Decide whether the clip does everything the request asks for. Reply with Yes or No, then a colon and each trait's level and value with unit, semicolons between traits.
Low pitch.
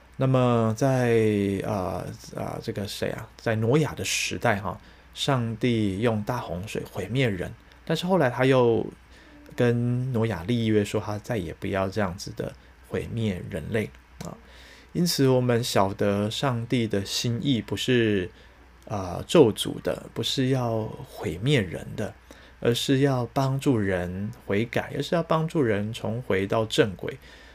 Yes: low, 115 Hz